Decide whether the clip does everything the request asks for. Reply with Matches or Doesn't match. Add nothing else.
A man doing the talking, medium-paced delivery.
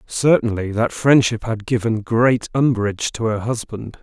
Matches